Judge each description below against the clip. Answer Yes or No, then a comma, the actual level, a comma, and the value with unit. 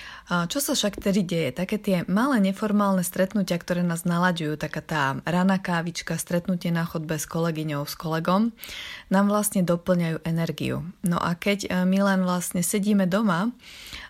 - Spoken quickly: No, average, 155 wpm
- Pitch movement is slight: No, average, 3.1 semitones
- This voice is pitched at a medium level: Yes, medium, 180 Hz